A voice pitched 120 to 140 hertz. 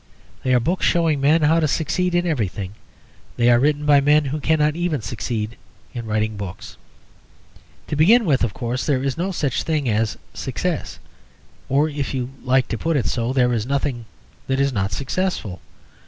Yes: low, 135 Hz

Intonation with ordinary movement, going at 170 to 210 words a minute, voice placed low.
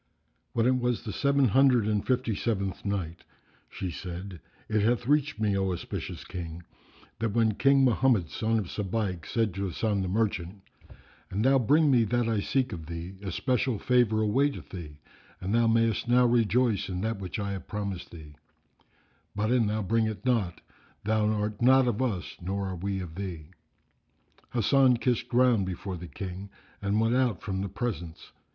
Yes: average, 4.2 semitones; average, 175 wpm; low, 105 Hz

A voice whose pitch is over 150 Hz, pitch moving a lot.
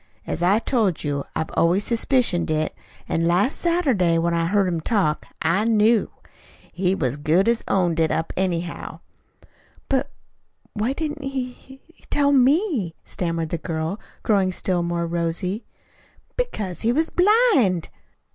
Yes: high, 190 Hz; wide, 7.1 semitones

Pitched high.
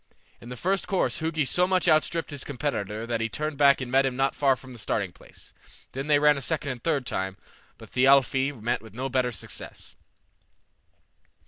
No: low, 135 Hz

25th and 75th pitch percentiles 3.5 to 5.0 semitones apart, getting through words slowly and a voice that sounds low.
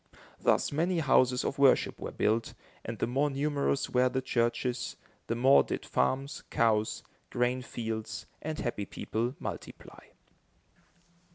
No: average, 2.8 semitones; slow, 130 wpm; low, 125 Hz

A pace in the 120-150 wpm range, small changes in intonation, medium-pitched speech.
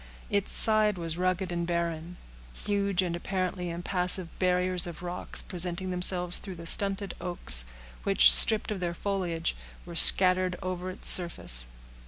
Yes: average, 145 wpm; narrow, 1.7 semitones; medium, 180 Hz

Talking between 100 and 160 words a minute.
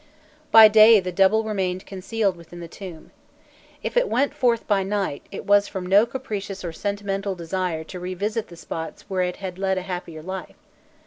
No: average, 185 wpm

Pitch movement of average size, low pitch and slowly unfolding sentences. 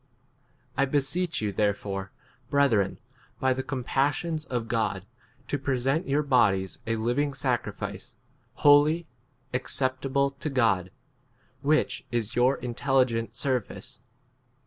Yes: average, 3.7 semitones; low, 130 Hz; slow, 120 wpm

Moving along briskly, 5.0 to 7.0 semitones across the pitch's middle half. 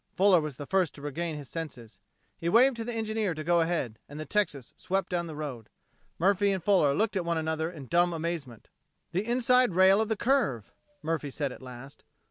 Yes: fast, 210 wpm; average, 5.3 semitones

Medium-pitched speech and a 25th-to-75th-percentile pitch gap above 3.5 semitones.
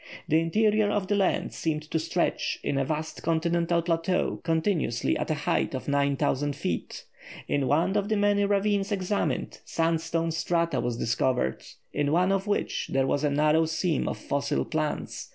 Yes: medium, 165 Hz; average, 4.5 semitones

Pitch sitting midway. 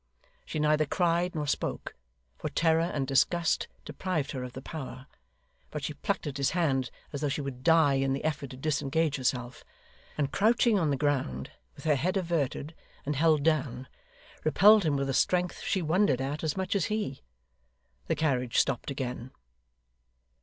Yes: medium, 150 Hz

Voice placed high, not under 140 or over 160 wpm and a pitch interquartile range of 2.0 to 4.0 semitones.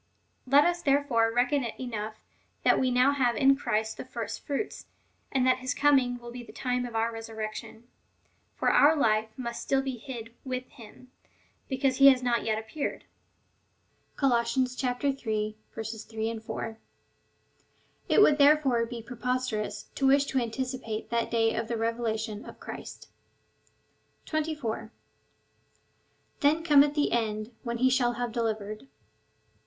Yes: high, 245 Hz; average, 150 wpm; average, 3.1 semitones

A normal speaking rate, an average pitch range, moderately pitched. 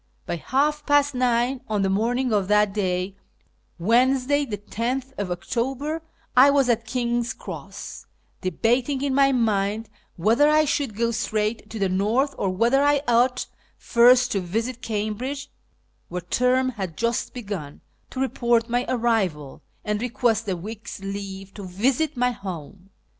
No: average, 145 wpm; average, 4.3 semitones; high, 235 Hz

